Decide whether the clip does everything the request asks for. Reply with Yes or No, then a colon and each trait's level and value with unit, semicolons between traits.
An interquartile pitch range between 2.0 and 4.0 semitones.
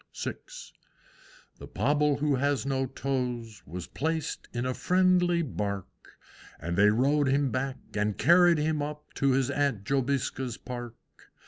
Yes: average, 3.7 semitones